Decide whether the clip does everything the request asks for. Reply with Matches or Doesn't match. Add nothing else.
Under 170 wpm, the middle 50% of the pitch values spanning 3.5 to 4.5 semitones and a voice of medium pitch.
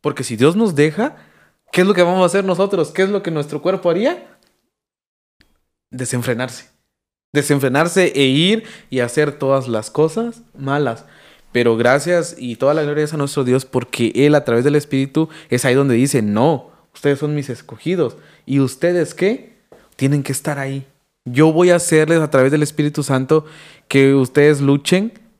Doesn't match